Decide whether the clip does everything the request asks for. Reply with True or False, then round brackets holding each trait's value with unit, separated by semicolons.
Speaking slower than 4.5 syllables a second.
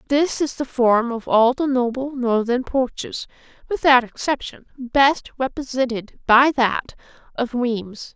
True (4.0 syllables/s)